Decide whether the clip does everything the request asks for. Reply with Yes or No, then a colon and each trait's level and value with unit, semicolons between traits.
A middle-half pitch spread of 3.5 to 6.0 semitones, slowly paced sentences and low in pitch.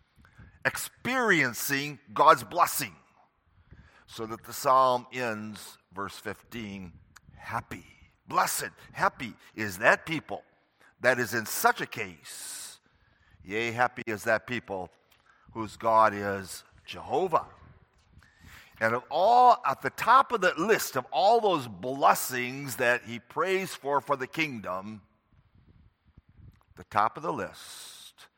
Yes: average, 4.0 semitones; slow, 120 wpm; low, 110 Hz